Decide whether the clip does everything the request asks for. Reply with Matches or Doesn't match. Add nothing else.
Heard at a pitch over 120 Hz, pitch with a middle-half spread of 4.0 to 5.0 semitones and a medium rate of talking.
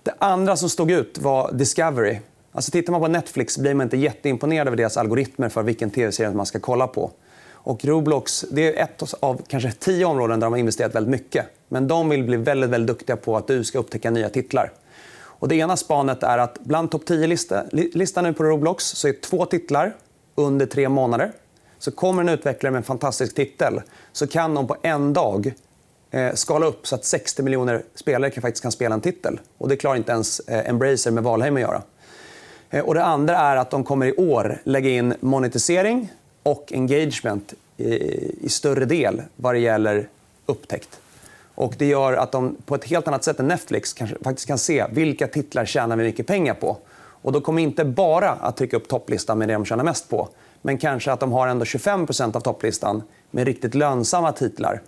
Doesn't match